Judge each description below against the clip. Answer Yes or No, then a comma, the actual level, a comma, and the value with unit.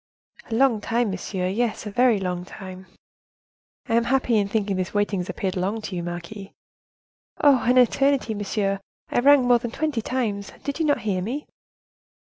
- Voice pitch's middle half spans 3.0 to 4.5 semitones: Yes, average, 4.2 semitones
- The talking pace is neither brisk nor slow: Yes, average, 185 wpm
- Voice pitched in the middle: No, high, 215 Hz